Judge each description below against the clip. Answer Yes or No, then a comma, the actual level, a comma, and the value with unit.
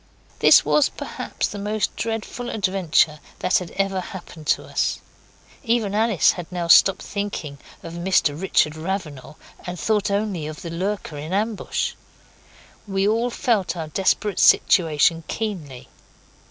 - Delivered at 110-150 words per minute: Yes, average, 140 wpm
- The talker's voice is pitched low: No, high, 190 Hz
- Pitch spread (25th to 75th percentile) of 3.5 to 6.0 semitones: Yes, average, 4.2 semitones